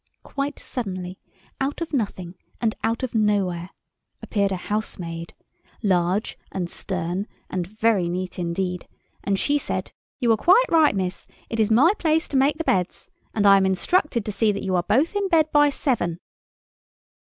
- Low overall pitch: No, high, 210 Hz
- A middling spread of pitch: No, wide, 6.8 semitones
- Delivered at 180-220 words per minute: No, average, 165 wpm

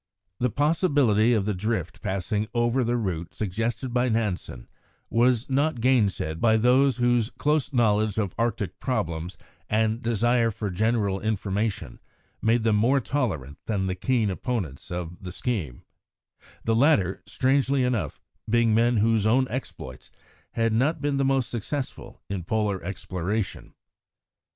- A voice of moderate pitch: No, low, 110 Hz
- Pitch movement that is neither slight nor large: Yes, average, 4.0 semitones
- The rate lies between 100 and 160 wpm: Yes, average, 140 wpm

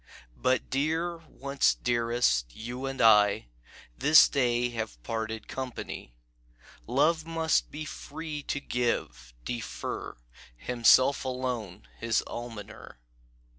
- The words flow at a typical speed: No, slow, 100 wpm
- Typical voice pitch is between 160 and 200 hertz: No, low, 125 Hz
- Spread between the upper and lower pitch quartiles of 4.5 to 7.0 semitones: No, average, 4.0 semitones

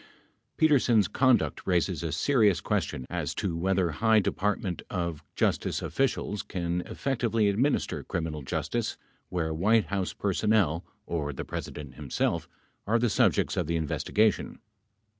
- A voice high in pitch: No, very low, 95 Hz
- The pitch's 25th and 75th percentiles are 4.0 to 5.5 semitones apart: Yes, average, 5.1 semitones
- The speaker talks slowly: Yes, slow, 130 wpm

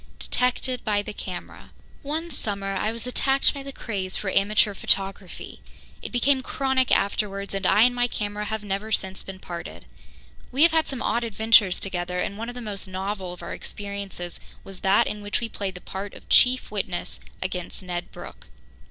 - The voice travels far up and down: No, average, 4.1 semitones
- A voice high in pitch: Yes, high, 205 Hz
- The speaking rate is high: No, average, 185 wpm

